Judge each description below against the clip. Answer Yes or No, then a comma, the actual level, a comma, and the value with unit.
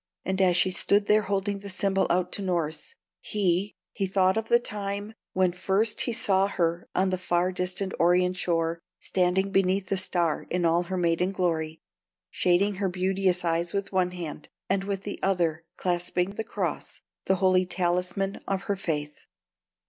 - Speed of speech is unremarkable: Yes, average, 170 wpm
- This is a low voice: No, medium, 185 Hz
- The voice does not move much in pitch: Yes, narrow, 1.9 semitones